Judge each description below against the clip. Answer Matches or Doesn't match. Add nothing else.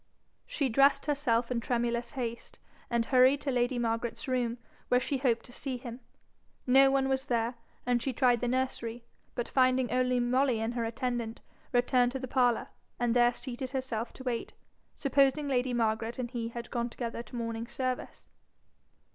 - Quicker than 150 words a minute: Matches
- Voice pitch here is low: Doesn't match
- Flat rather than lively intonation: Matches